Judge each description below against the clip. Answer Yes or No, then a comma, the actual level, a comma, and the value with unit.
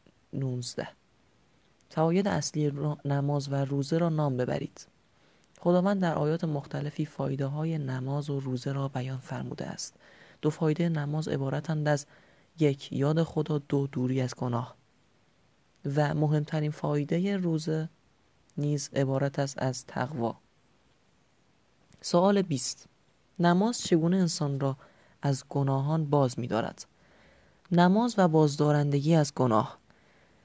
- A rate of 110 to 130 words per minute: Yes, average, 115 wpm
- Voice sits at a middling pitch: Yes, medium, 150 Hz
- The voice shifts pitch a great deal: No, average, 2.8 semitones